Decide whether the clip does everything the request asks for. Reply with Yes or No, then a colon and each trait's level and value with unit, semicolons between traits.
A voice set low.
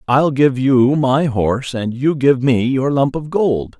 Yes: low, 130 Hz